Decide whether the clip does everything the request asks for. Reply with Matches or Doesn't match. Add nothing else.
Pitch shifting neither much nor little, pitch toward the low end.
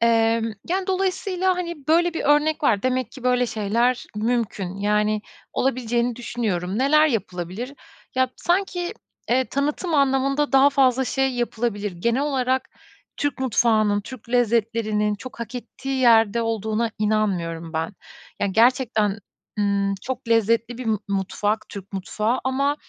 Doesn't match